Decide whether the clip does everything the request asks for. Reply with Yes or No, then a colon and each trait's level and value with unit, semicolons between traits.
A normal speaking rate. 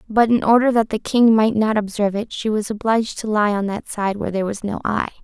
No: fast, 265 wpm